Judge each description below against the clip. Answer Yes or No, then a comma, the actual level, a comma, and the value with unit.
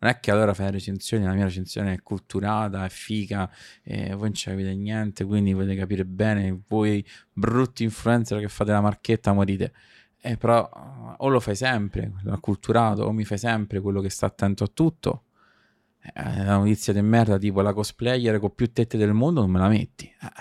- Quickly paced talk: Yes, fast, 205 wpm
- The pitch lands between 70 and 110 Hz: Yes, low, 105 Hz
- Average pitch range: No, narrow, 2.3 semitones